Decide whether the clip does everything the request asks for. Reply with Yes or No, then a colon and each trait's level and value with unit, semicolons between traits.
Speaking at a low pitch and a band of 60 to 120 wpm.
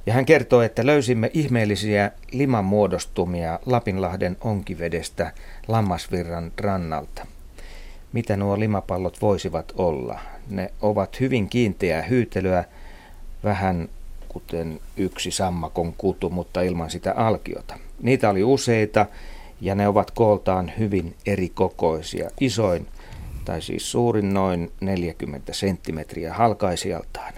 Yes: very low, 95 Hz; average, 105 wpm